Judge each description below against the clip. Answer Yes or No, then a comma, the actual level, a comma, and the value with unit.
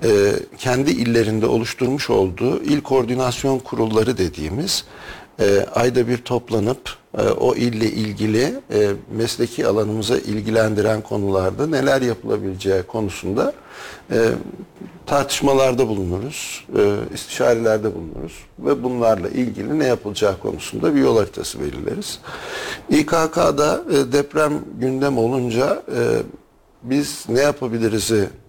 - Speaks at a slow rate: Yes, slow, 90 wpm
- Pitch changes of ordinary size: Yes, average, 4.0 semitones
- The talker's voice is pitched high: No, low, 120 Hz